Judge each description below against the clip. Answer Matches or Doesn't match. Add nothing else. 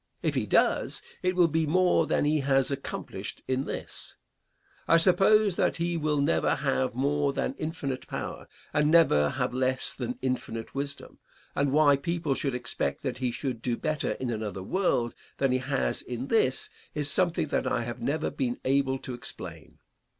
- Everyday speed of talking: Matches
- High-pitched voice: Doesn't match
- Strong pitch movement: Doesn't match